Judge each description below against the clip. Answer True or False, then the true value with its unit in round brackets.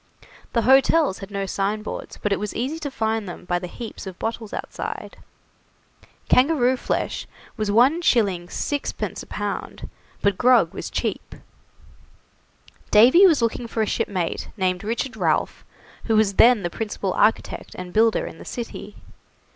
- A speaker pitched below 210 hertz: False (220 Hz)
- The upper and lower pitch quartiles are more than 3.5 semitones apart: True (4.0 semitones)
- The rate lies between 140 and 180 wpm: True (150 wpm)